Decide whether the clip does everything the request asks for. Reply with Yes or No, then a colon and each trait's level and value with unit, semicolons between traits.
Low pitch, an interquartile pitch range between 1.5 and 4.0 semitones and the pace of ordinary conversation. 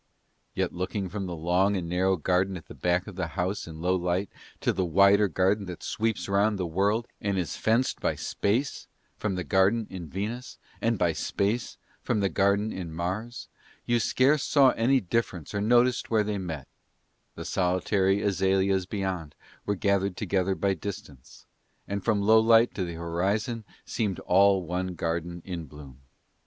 Yes: very low, 95 Hz; average, 2.8 semitones; average, 170 wpm